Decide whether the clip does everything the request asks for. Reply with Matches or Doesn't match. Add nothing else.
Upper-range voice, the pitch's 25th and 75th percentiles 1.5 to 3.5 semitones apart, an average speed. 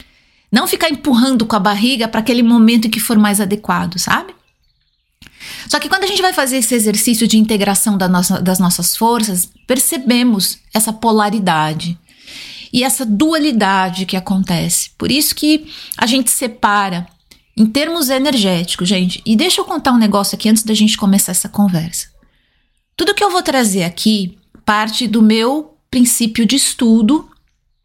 Doesn't match